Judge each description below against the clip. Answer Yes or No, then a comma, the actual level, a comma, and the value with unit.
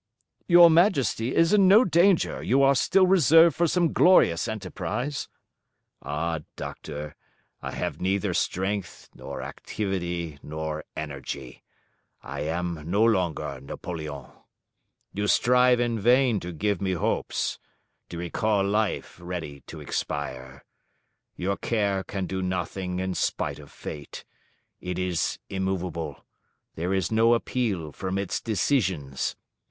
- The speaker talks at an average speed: No, slow, 125 wpm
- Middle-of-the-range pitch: No, very low, 95 Hz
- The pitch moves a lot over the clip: Yes, wide, 6.4 semitones